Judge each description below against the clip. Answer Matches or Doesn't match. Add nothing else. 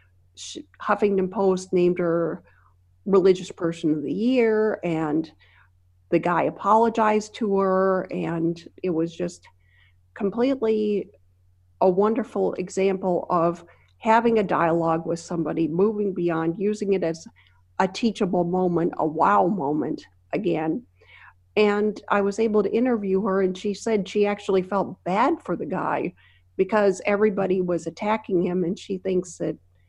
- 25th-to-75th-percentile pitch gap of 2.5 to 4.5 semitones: Matches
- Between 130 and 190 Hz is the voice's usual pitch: Matches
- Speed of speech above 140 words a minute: Doesn't match